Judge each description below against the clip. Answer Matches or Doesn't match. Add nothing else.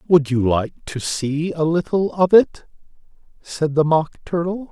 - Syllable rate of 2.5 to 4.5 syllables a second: Matches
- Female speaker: Doesn't match